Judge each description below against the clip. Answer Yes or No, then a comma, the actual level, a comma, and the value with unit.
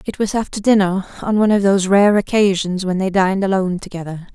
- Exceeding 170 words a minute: Yes, fast, 205 wpm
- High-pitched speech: Yes, high, 195 Hz